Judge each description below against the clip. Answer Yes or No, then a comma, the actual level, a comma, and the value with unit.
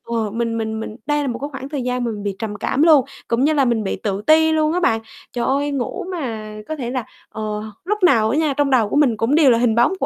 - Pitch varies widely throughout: No, average, 4.8 semitones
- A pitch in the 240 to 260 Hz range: Yes, very high, 250 Hz